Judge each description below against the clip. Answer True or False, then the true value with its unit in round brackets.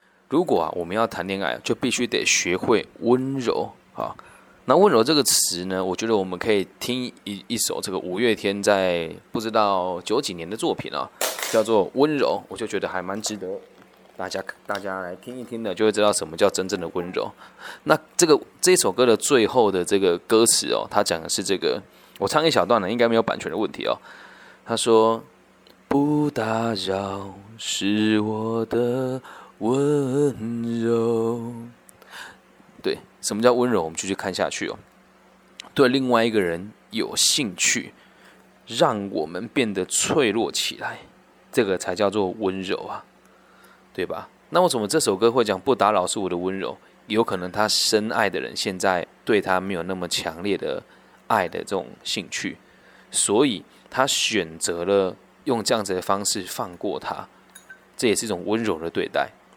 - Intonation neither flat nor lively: True (3.8 semitones)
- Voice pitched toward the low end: True (110 Hz)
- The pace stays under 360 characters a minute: True (245 characters per minute)